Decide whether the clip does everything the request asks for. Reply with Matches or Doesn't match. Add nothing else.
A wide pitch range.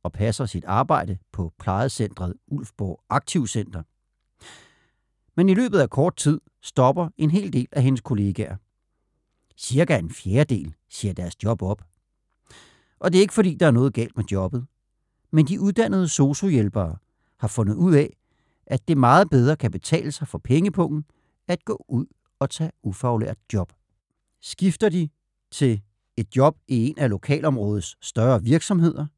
Matches